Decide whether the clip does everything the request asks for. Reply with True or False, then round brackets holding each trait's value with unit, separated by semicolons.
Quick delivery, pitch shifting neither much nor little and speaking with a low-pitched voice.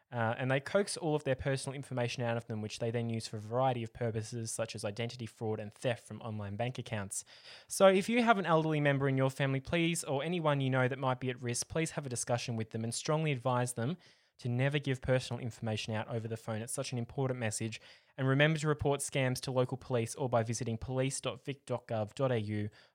True (225 wpm; 3.2 semitones; 125 Hz)